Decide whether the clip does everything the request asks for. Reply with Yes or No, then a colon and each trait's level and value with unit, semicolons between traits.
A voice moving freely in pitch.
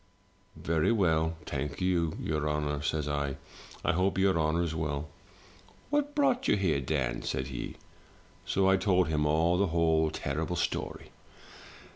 No: average, 3.7 semitones